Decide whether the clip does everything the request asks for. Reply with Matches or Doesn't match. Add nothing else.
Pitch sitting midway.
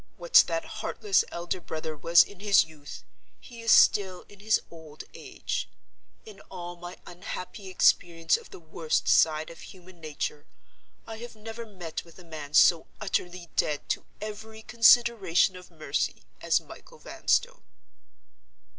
Matches